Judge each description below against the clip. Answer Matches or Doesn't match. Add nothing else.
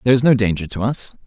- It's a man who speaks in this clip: Matches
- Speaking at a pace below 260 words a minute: Doesn't match